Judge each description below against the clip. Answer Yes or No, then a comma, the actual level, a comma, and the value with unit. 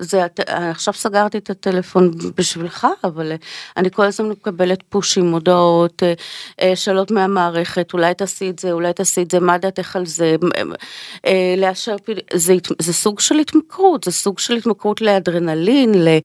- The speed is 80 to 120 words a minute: No, average, 145 wpm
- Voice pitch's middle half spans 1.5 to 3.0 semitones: Yes, narrow, 2.5 semitones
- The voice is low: No, medium, 185 Hz